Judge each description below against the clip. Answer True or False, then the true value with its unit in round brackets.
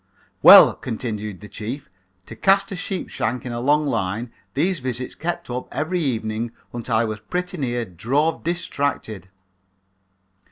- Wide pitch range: True (6.2 semitones)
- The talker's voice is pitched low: True (125 Hz)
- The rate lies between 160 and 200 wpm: False (150 wpm)